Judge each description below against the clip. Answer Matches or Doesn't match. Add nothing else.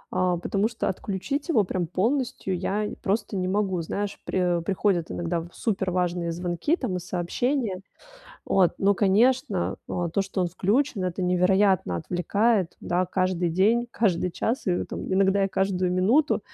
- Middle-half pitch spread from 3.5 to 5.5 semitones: Doesn't match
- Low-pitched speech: Doesn't match